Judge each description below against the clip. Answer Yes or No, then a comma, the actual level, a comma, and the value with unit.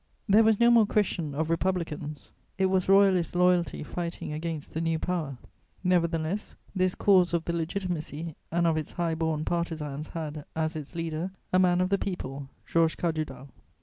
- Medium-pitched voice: Yes, medium, 170 Hz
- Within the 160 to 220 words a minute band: Yes, average, 170 wpm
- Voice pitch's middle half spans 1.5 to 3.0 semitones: Yes, narrow, 2.6 semitones